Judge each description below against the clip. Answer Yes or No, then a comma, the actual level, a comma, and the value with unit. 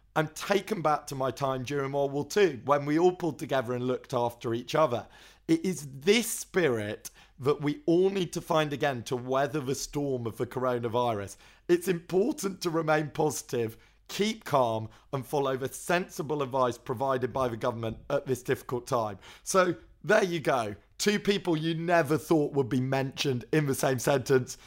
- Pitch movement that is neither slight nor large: Yes, average, 4.5 semitones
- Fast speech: No, average, 180 wpm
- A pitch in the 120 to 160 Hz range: Yes, medium, 140 Hz